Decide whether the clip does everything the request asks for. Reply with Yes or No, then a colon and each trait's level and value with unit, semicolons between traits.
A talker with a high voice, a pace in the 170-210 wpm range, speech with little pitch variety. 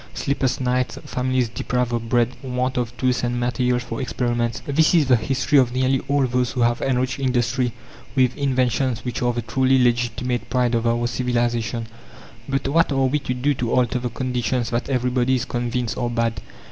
No: low, 125 Hz; average, 185 wpm; narrow, 1.4 semitones